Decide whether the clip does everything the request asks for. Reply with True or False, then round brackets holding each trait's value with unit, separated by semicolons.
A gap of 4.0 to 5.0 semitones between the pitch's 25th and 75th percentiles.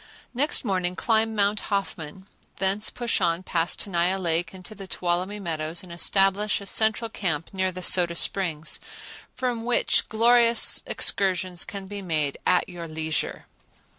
False (3.4 semitones)